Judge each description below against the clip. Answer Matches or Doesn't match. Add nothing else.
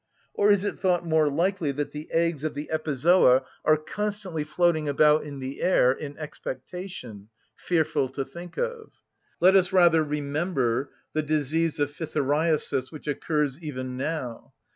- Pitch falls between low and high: Matches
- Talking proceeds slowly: Doesn't match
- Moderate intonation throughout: Matches